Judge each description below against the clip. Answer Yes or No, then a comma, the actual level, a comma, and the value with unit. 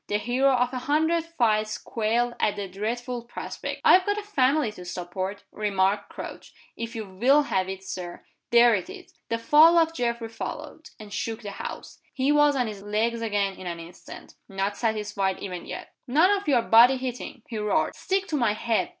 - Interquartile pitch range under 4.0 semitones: No, average, 4.7 semitones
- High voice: Yes, high, 230 Hz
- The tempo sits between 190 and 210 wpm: Yes, average, 195 wpm